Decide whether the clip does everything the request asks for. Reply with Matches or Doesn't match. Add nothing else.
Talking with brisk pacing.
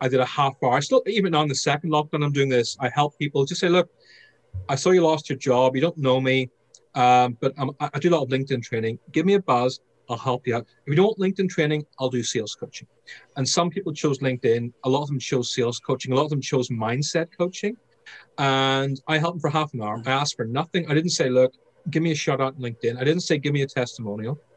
Matches